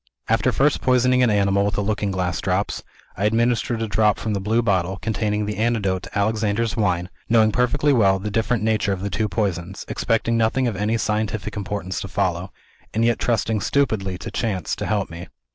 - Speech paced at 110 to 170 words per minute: No, average, 195 wpm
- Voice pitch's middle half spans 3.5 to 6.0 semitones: No, average, 2.8 semitones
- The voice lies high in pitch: No, low, 105 Hz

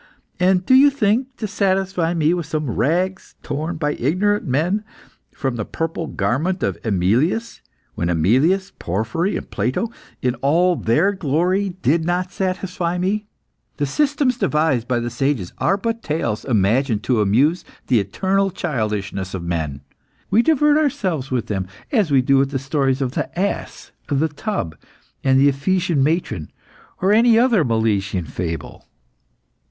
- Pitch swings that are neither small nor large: No, wide, 7.9 semitones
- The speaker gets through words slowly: No, average, 150 wpm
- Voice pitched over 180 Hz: No, medium, 155 Hz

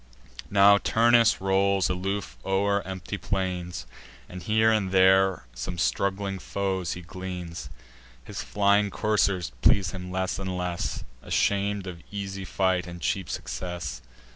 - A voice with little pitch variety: Yes, narrow, 1.7 semitones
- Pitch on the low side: Yes, very low, 95 Hz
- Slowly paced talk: Yes, slow, 130 wpm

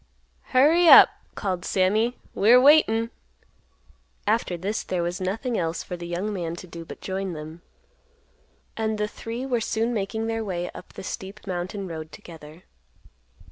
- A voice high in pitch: Yes, high, 195 Hz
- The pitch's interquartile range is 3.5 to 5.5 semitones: Yes, average, 4.4 semitones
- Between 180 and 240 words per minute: No, average, 155 wpm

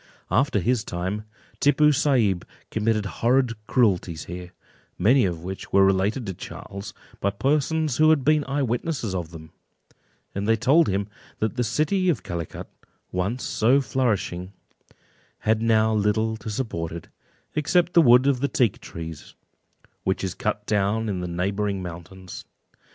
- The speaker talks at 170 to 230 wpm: No, average, 150 wpm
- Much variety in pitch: Yes, wide, 5.7 semitones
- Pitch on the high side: No, low, 110 Hz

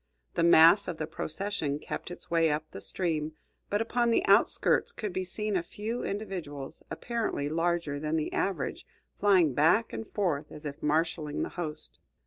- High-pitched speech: No, medium, 170 Hz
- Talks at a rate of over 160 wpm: Yes, average, 170 wpm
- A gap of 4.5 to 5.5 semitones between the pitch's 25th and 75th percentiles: Yes, average, 5.0 semitones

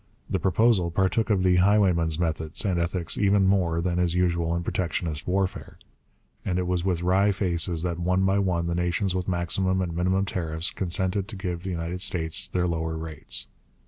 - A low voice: Yes, very low, 90 Hz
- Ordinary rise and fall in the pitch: No, narrow, 2.0 semitones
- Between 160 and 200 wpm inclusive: Yes, average, 185 wpm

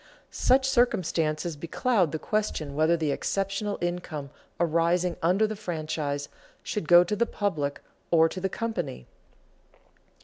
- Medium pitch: Yes, medium, 175 Hz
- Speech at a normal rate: No, slow, 130 wpm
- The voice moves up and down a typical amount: Yes, average, 4.6 semitones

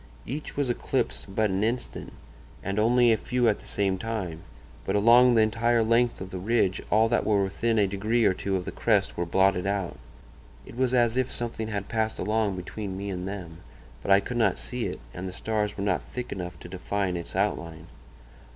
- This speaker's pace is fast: Yes, fast, 210 wpm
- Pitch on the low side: Yes, low, 105 Hz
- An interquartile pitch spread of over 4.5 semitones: No, average, 3.5 semitones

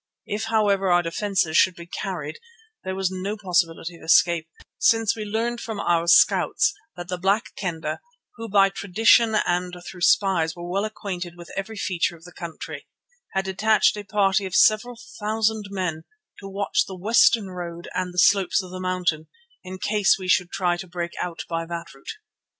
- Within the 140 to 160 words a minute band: No, average, 180 wpm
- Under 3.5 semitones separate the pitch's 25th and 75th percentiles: Yes, average, 2.9 semitones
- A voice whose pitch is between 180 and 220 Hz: Yes, medium, 185 Hz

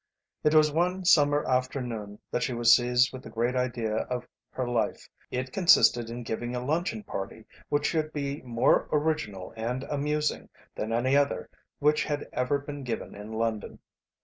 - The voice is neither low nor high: No, low, 130 Hz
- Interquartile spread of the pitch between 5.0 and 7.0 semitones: No, average, 3.9 semitones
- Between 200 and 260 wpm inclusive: No, average, 170 wpm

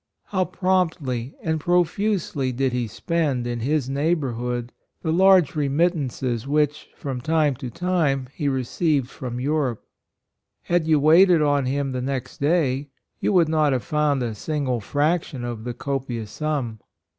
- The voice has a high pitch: No, medium, 140 Hz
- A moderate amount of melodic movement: Yes, average, 4.1 semitones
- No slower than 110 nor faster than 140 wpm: No, average, 150 wpm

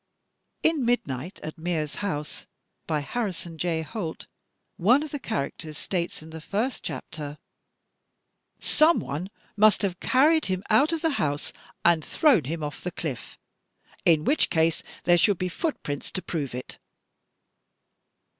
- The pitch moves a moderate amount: No, wide, 6.7 semitones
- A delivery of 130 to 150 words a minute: Yes, average, 145 wpm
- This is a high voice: No, medium, 175 Hz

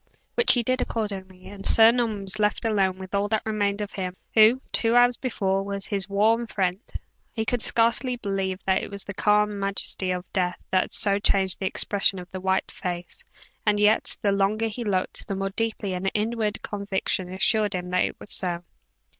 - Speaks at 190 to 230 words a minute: Yes, average, 195 wpm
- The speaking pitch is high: Yes, high, 200 Hz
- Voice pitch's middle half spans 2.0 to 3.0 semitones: Yes, narrow, 2.4 semitones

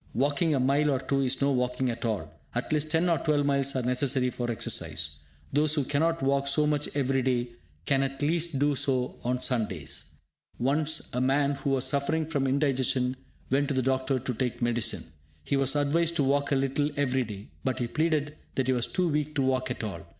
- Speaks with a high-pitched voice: No, low, 135 Hz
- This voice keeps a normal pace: No, fast, 210 wpm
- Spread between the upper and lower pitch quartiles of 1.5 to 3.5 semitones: Yes, narrow, 2.4 semitones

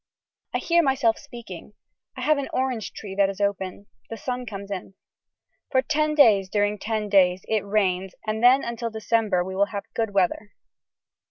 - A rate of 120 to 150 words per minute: No, average, 175 wpm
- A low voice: No, high, 215 Hz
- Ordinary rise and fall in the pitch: Yes, average, 3.6 semitones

